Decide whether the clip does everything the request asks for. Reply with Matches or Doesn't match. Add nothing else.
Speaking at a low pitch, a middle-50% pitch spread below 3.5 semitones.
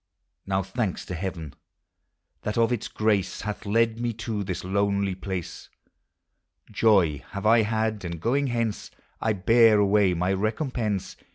Matches